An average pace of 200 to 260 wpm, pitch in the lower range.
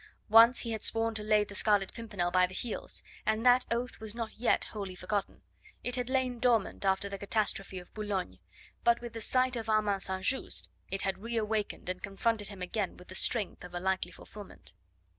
No: fast, 205 wpm; high, 210 Hz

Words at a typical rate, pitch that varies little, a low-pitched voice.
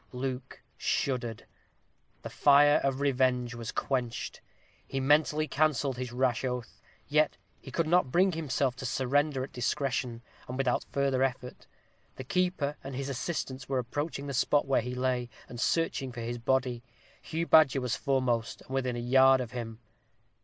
Yes: average, 160 wpm; narrow, 2.3 semitones; low, 130 Hz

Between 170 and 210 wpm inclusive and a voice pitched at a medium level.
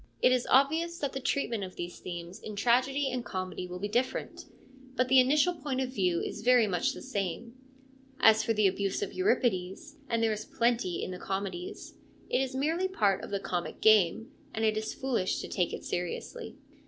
No: average, 200 wpm; high, 225 Hz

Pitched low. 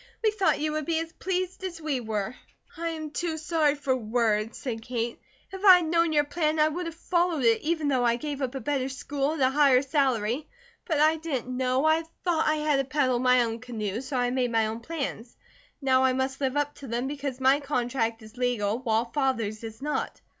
No: very high, 270 Hz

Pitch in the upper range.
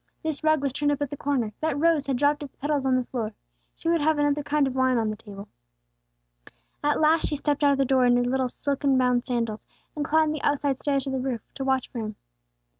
Yes: very high, 275 Hz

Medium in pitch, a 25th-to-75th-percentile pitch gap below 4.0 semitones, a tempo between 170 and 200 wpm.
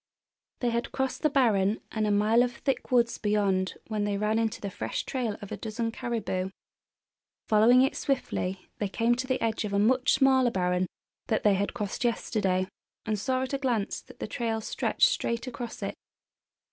No: high, 225 Hz; average, 3.4 semitones; average, 190 wpm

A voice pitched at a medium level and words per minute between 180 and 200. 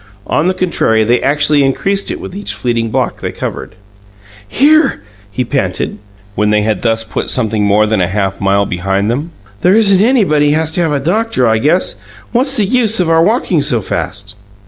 Yes: medium, 145 Hz; average, 190 wpm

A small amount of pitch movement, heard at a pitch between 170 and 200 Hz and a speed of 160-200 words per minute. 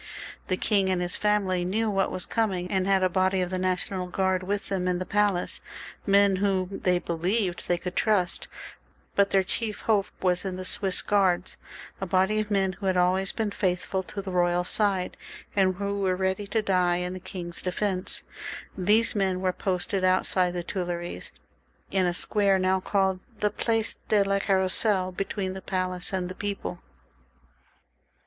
Yes: narrow, 1.6 semitones; high, 190 Hz; average, 180 wpm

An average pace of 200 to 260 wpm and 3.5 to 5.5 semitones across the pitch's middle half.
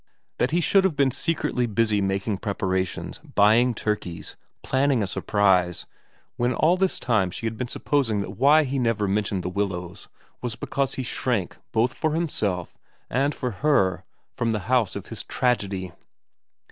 No: average, 160 wpm; average, 5.2 semitones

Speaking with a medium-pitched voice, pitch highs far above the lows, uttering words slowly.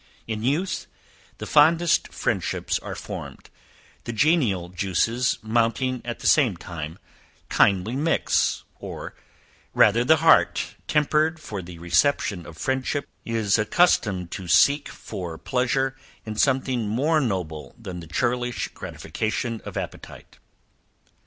No: low, 115 Hz; wide, 6.3 semitones; slow, 120 wpm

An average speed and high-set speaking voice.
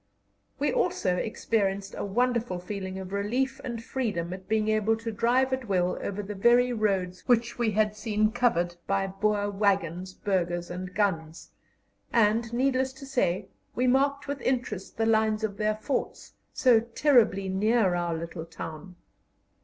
Yes: average, 155 wpm; high, 215 Hz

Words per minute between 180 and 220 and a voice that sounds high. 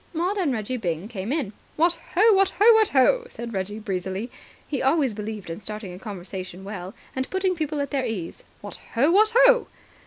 Yes: average, 195 wpm; very high, 250 Hz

